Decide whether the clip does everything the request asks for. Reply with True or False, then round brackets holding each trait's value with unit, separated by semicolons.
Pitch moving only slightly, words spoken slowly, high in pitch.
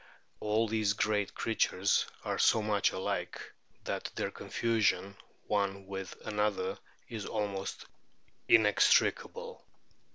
False (1.9 semitones; 105 wpm; 105 Hz)